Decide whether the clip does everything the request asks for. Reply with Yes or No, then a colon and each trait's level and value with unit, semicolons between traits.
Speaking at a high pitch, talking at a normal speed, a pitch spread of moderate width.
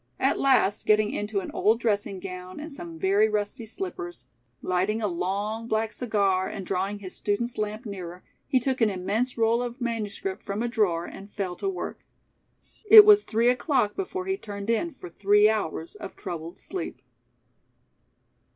Yes: high, 215 Hz; average, 170 wpm; average, 3.8 semitones